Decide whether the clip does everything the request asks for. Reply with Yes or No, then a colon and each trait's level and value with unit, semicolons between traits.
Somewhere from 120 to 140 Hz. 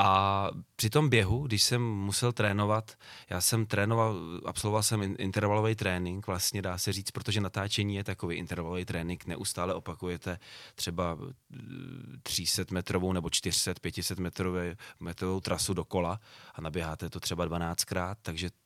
No: very low, 95 Hz